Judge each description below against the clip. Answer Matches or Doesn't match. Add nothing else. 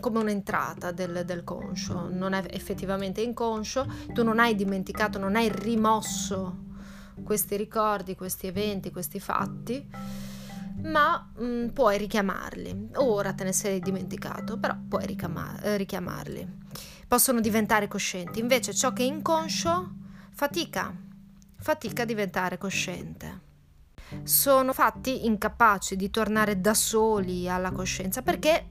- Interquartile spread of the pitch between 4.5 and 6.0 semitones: Doesn't match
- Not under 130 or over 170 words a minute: Doesn't match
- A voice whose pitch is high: Matches